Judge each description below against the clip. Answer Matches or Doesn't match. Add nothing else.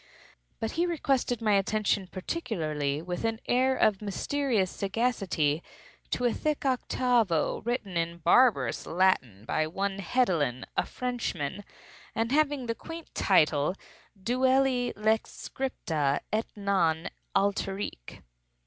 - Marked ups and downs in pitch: Matches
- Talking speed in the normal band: Doesn't match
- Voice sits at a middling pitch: Doesn't match